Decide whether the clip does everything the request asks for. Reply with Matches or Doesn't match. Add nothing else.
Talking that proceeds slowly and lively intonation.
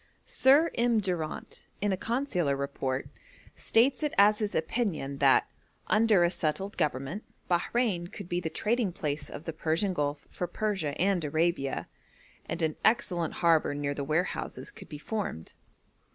Doesn't match